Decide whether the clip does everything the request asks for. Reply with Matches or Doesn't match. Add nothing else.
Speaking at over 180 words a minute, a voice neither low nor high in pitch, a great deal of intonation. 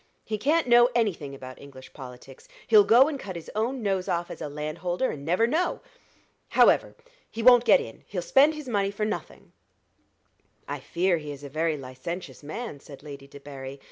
Matches